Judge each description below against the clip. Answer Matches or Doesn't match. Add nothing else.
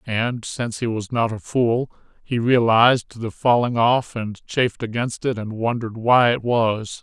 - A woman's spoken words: Doesn't match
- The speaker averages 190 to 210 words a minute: Doesn't match